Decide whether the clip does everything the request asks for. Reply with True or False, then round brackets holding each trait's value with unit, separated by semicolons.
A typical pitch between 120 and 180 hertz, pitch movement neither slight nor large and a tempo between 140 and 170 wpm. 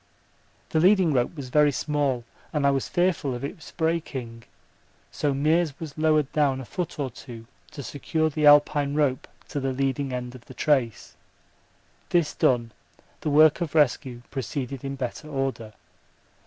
True (140 Hz; 3.0 semitones; 160 wpm)